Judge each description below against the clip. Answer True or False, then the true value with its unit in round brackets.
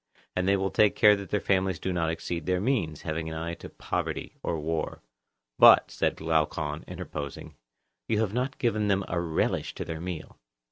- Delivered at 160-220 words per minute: True (190 wpm)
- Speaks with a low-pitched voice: True (85 Hz)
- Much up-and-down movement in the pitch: False (3.7 semitones)